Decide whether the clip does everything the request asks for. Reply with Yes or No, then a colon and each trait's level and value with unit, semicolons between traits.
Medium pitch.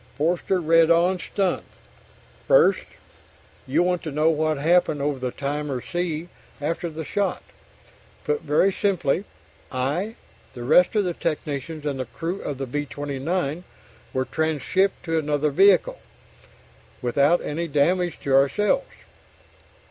Yes: medium, 160 Hz